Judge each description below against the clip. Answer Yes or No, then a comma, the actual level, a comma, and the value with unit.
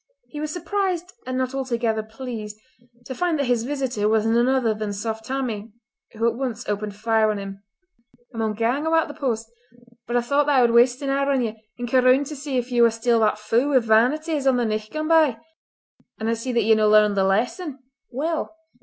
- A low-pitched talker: No, high, 240 Hz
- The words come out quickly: Yes, fast, 235 wpm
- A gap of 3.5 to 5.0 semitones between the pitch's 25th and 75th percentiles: Yes, average, 3.8 semitones